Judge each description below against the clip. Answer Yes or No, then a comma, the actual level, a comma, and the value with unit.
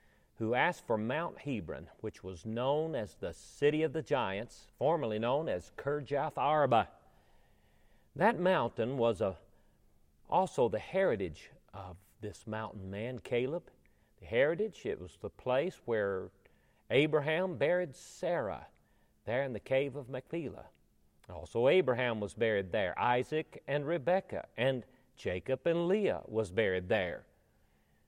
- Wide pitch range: Yes, wide, 7.5 semitones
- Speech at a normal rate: No, slow, 130 wpm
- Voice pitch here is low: Yes, low, 125 Hz